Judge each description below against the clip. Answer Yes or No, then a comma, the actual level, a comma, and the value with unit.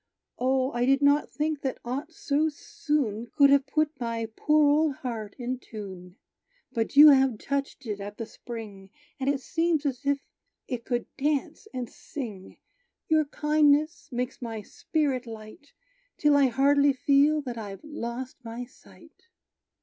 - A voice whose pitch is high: Yes, very high, 270 Hz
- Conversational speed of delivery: Yes, average, 155 wpm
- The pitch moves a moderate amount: Yes, average, 3.9 semitones